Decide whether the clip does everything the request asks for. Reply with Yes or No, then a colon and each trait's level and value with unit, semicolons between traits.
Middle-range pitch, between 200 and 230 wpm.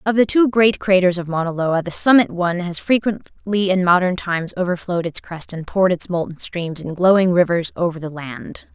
Yes: medium, 180 Hz; fast, 205 wpm